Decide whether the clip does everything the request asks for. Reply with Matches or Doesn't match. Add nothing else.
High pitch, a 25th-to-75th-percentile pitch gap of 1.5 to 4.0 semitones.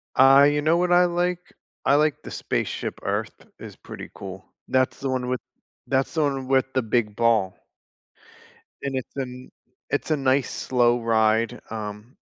Doesn't match